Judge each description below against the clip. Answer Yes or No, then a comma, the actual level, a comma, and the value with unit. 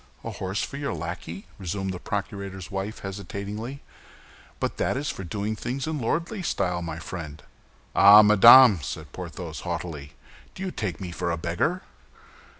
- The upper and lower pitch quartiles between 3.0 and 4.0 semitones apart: No, average, 5.1 semitones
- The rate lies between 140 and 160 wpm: Yes, average, 150 wpm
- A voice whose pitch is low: Yes, low, 100 Hz